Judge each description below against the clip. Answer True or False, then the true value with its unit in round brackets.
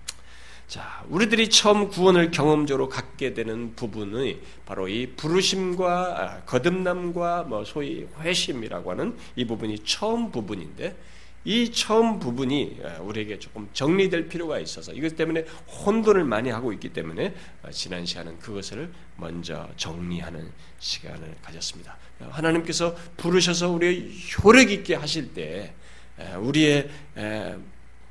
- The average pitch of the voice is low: False (150 Hz)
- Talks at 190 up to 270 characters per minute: False (290 characters per minute)